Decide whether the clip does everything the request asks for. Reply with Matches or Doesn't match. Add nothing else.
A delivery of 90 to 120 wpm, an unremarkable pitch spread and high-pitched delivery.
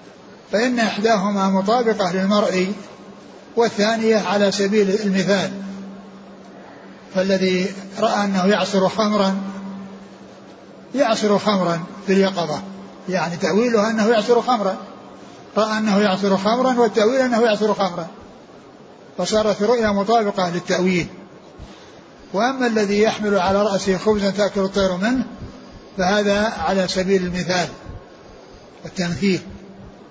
Doesn't match